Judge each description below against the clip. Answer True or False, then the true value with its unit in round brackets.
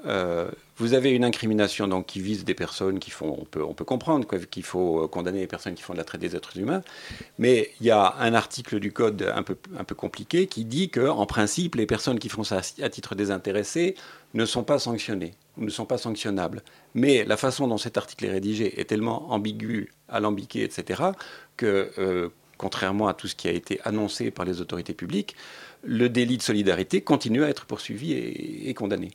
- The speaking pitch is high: False (105 Hz)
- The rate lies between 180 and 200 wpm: False (215 wpm)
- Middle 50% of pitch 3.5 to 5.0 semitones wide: True (3.8 semitones)